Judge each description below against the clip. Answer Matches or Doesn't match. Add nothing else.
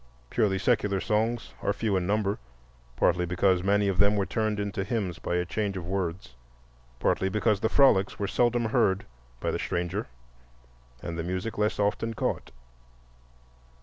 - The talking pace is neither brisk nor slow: Matches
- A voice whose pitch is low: Matches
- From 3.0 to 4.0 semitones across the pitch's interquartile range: Doesn't match